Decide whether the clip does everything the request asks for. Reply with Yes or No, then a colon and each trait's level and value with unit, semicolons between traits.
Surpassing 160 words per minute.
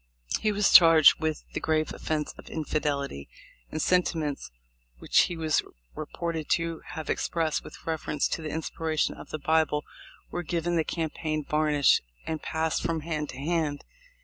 No: average, 155 wpm